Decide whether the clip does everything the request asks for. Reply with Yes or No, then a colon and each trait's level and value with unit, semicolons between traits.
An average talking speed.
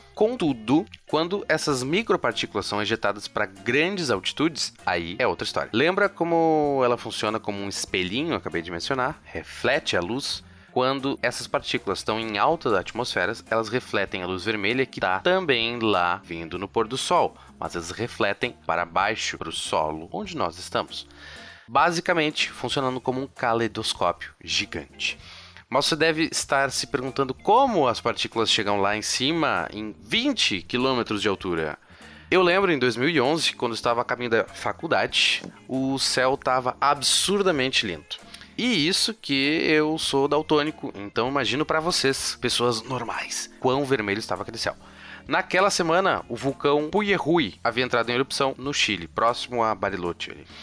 Yes: average, 155 wpm